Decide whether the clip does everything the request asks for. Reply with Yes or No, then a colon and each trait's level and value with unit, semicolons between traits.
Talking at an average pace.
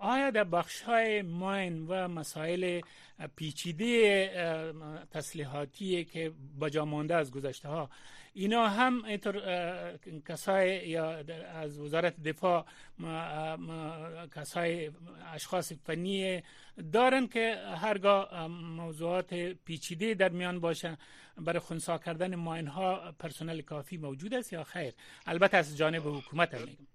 Yes: average, 115 wpm